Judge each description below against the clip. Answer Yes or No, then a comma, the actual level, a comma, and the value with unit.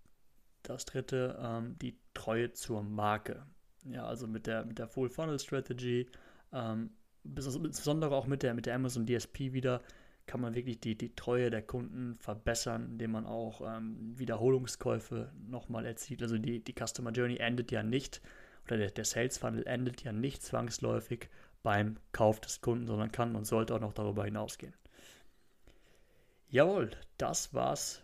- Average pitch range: No, narrow, 2.1 semitones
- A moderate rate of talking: Yes, average, 150 wpm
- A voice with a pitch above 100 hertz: Yes, low, 120 Hz